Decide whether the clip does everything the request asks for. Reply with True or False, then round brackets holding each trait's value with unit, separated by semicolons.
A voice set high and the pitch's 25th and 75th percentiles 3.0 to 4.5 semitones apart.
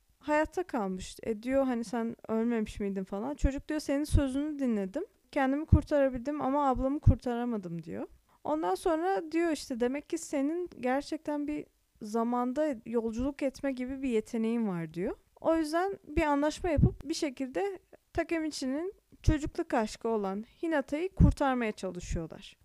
False (275 Hz; 5.0 semitones)